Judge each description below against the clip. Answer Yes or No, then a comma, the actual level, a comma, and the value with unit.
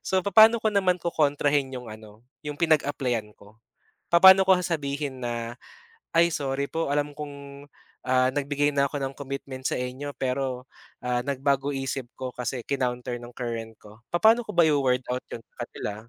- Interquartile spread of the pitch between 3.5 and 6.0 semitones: No, average, 2.9 semitones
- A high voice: No, medium, 140 Hz